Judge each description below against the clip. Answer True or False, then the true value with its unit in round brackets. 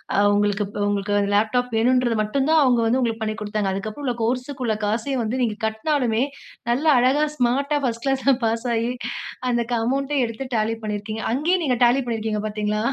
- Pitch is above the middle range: True (235 Hz)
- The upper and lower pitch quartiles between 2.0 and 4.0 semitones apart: True (3.3 semitones)